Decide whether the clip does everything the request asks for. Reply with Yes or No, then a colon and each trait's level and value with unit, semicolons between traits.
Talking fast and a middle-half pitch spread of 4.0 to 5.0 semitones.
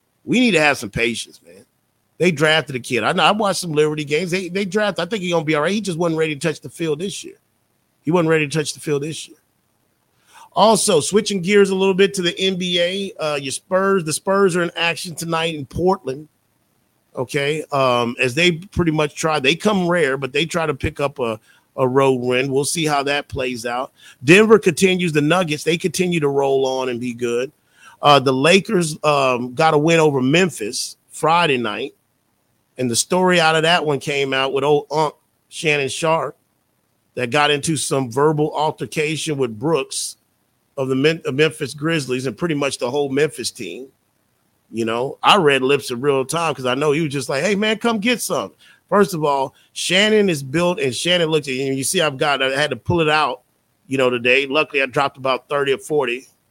Yes: fast, 215 wpm; average, 4.5 semitones